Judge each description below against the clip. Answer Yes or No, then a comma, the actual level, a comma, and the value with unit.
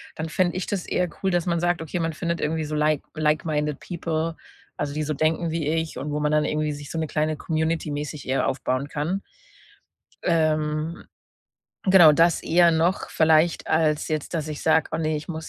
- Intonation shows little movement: Yes, narrow, 1.7 semitones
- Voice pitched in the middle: Yes, medium, 155 Hz